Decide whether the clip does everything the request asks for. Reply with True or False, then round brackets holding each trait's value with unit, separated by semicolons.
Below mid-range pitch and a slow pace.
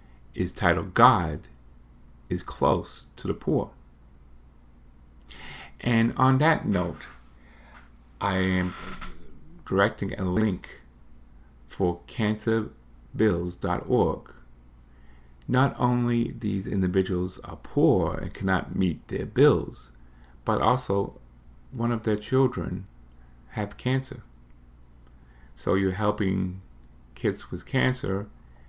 True (85 Hz; 90 wpm)